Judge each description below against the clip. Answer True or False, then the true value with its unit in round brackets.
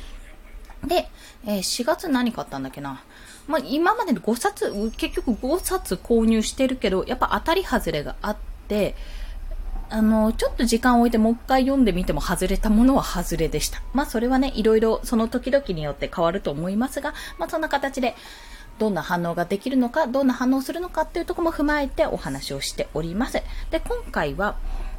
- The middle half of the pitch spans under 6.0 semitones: False (7.3 semitones)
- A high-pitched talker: True (235 Hz)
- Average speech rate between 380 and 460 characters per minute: False (365 characters per minute)